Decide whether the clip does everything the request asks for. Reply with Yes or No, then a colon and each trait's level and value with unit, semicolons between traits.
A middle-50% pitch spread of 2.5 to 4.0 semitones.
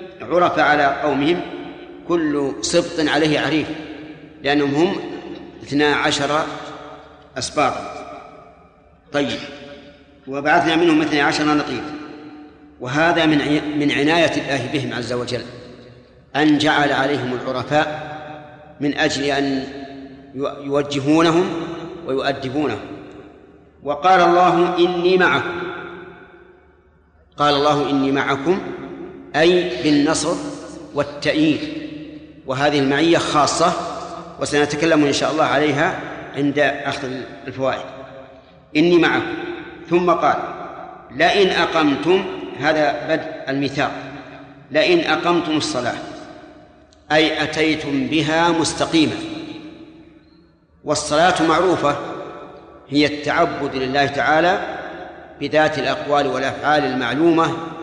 Yes: average, 3.5 semitones